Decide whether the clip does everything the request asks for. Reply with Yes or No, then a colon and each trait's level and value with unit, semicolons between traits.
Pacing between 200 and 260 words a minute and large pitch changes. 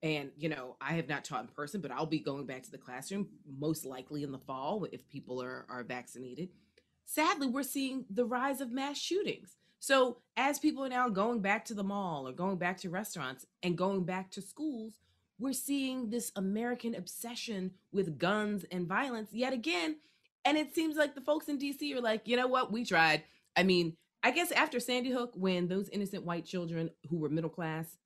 Yes: fast, 205 wpm; wide, 7.5 semitones